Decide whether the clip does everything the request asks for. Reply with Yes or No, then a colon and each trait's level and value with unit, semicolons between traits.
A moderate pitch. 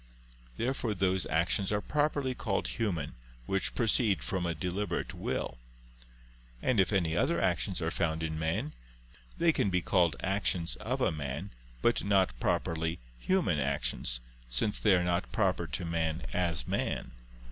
No: very low, 90 Hz